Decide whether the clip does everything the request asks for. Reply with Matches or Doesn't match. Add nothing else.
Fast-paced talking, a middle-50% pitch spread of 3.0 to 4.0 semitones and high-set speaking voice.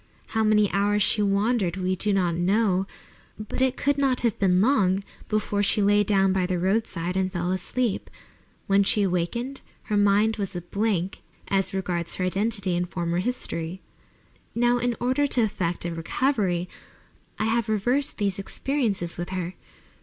Doesn't match